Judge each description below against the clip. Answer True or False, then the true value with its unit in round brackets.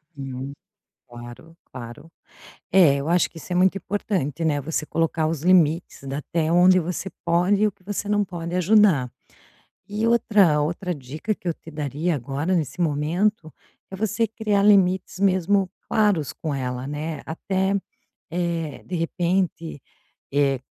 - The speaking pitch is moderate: True (170 Hz)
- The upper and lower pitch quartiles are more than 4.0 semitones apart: True (4.4 semitones)